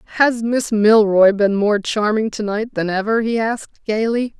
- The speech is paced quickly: No, average, 180 wpm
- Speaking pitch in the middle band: No, high, 215 Hz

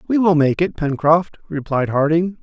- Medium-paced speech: Yes, average, 175 wpm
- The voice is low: No, medium, 160 Hz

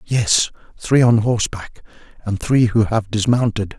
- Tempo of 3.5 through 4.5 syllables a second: Yes, 4.4 syllables/s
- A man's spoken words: Yes, male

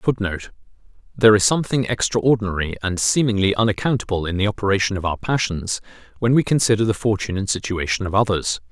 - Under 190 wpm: Yes, average, 160 wpm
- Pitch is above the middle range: No, low, 105 Hz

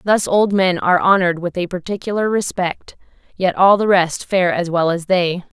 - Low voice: No, medium, 185 Hz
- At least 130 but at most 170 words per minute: No, average, 195 wpm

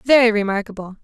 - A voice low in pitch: No, high, 215 Hz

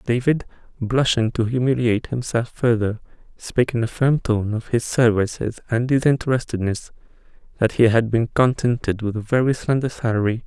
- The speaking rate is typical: Yes, average, 145 wpm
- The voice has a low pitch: Yes, low, 120 Hz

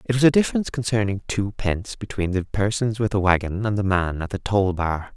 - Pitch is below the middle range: Yes, low, 100 Hz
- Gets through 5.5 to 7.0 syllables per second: Yes, 5.8 syllables/s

